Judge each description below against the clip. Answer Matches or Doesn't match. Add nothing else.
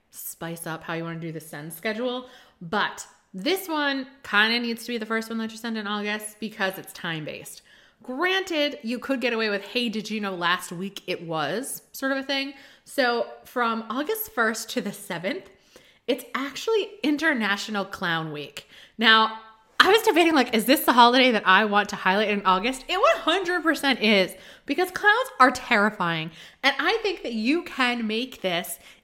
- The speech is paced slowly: Doesn't match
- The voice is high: Matches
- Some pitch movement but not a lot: Doesn't match